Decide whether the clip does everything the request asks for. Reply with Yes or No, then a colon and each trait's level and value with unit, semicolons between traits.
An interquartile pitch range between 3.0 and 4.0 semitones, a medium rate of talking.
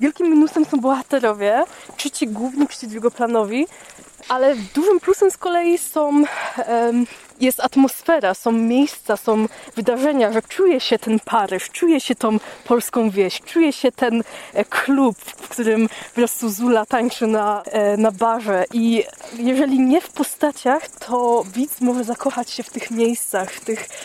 No: average, 4.4 semitones; average, 150 wpm